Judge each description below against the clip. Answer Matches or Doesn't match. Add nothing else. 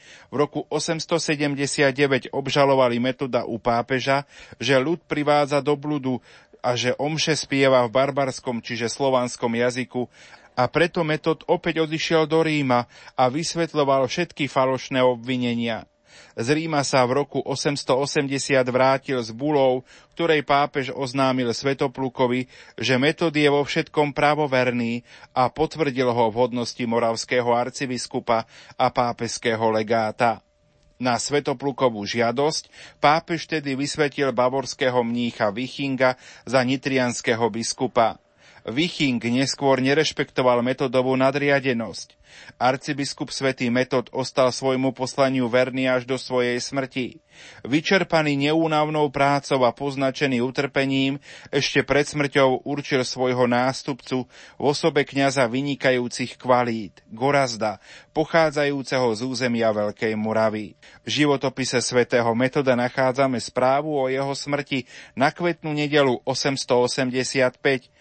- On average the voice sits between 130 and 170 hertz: Matches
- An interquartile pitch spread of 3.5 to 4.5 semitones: Doesn't match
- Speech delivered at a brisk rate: Doesn't match